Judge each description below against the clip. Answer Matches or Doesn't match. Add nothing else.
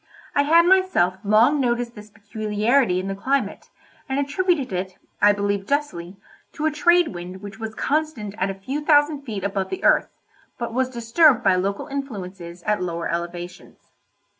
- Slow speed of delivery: Doesn't match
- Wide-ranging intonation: Matches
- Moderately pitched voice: Doesn't match